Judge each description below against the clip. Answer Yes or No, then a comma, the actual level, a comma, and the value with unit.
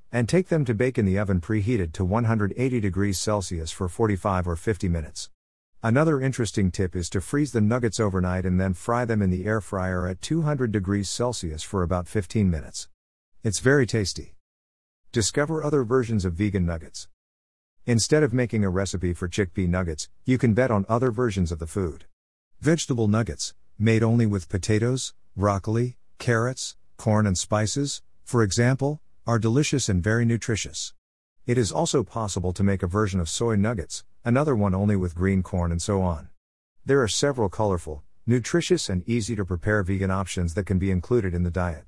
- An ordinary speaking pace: Yes, average, 180 wpm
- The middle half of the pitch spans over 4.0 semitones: Yes, average, 4.6 semitones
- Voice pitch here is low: Yes, low, 100 Hz